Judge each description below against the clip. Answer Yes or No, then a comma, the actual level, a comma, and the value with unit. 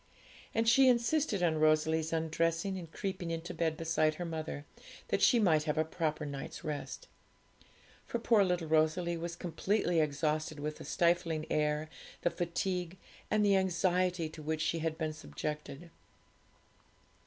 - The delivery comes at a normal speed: Yes, average, 150 wpm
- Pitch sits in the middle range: Yes, medium, 165 Hz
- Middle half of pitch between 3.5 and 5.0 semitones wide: No, narrow, 2.5 semitones